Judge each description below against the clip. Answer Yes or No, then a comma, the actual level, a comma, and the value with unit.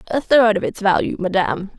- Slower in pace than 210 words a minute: Yes, average, 200 wpm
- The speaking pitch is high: Yes, high, 200 Hz